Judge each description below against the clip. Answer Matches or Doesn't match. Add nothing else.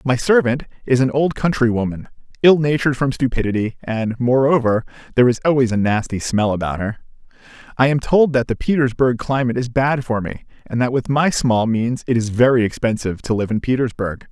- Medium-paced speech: Matches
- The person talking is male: Matches